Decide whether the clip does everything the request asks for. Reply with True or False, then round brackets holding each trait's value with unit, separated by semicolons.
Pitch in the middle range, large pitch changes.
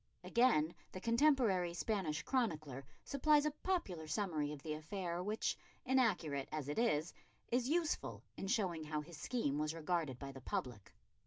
True (175 Hz; 7.5 semitones)